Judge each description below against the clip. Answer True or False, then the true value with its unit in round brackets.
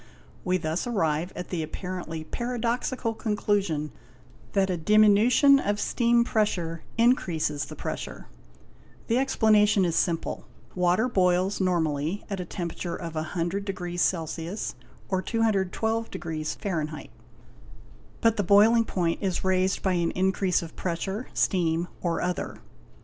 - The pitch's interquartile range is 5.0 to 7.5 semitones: False (4.1 semitones)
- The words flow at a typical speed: False (120 wpm)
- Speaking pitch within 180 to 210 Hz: True (185 Hz)